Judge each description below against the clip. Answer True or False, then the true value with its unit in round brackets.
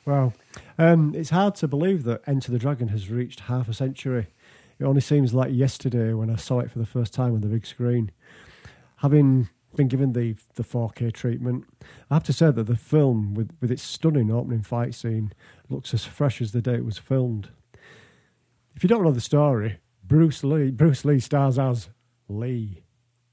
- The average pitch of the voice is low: True (125 Hz)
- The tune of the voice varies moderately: True (3.3 semitones)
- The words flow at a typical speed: True (195 wpm)